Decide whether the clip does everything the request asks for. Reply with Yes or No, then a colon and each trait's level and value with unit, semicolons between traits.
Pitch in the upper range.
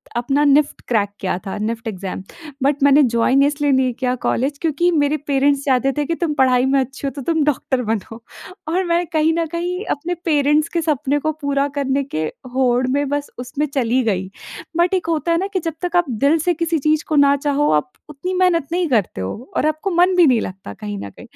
Yes: very high, 285 Hz